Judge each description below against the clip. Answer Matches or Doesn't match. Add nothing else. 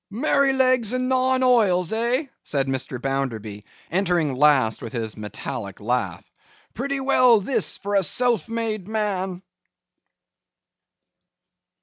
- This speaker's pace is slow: Matches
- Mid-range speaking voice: Doesn't match